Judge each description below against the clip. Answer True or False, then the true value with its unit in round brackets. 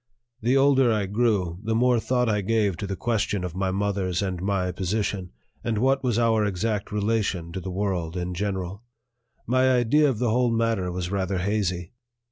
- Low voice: True (105 Hz)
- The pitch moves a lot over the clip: False (3.6 semitones)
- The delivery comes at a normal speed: True (185 wpm)